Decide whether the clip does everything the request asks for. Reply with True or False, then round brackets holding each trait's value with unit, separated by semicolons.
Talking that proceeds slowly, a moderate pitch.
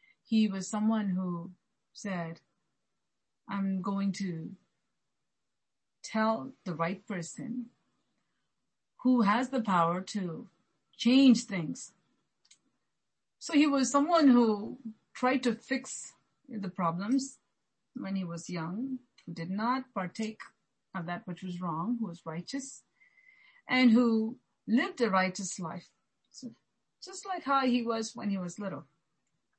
False (125 wpm; 220 Hz)